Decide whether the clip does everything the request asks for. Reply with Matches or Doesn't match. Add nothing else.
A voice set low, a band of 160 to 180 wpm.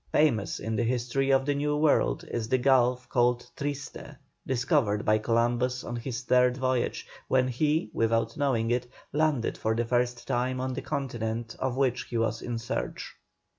Matches